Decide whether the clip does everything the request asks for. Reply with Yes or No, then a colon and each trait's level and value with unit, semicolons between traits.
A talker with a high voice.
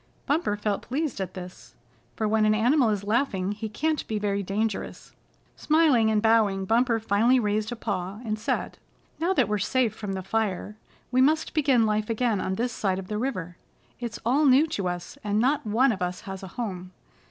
Yes: high, 215 Hz